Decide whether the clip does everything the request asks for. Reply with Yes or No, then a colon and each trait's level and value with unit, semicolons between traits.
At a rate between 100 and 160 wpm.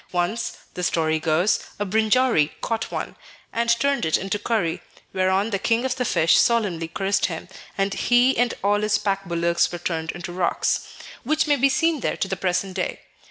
No: average, 190 wpm